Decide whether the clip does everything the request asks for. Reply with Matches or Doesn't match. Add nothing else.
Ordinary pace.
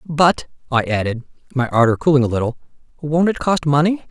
Matches